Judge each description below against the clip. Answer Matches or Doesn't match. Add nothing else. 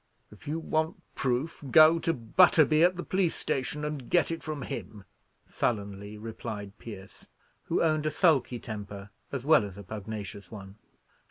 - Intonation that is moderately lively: Doesn't match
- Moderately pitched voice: Doesn't match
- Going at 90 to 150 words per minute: Doesn't match